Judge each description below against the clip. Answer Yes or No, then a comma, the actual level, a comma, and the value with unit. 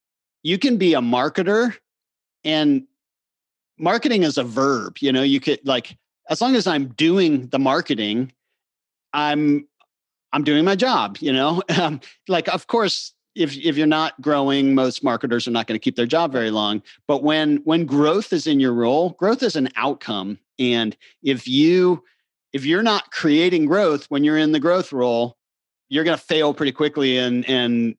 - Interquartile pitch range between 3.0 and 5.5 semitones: Yes, average, 4.7 semitones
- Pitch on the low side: No, medium, 145 Hz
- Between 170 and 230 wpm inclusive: Yes, average, 175 wpm